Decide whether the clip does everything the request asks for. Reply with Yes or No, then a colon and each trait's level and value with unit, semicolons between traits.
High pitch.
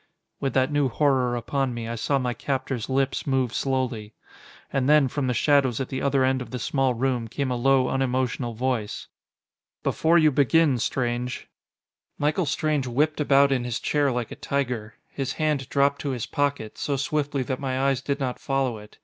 No: low, 135 Hz